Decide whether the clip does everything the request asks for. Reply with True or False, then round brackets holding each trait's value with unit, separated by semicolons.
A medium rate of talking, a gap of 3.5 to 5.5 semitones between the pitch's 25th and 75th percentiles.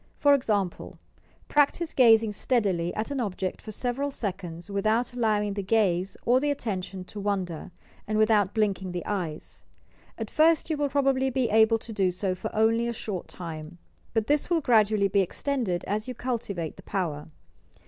True (180 wpm; 4.6 semitones)